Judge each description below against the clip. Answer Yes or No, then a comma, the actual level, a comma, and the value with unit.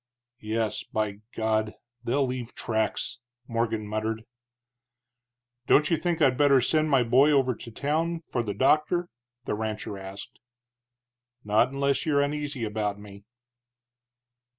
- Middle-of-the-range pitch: No, low, 120 Hz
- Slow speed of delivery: Yes, slow, 130 wpm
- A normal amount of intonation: Yes, average, 4.9 semitones